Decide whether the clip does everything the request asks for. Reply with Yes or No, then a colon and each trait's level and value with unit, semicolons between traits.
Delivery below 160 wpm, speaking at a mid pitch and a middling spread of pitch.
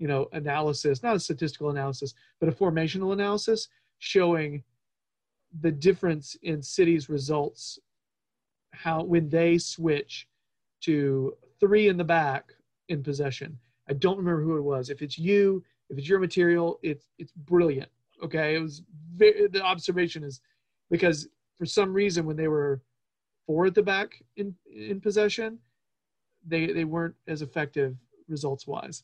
Yes: average, 150 wpm; medium, 165 Hz; average, 4.1 semitones